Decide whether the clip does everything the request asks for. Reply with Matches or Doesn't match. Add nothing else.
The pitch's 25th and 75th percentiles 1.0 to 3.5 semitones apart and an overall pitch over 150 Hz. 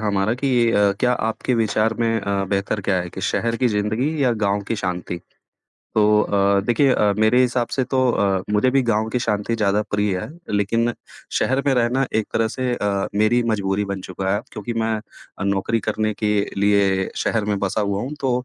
Doesn't match